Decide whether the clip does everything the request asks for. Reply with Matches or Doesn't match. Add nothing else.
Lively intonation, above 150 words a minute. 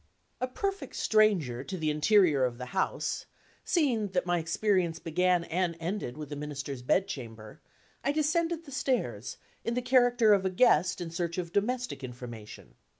Matches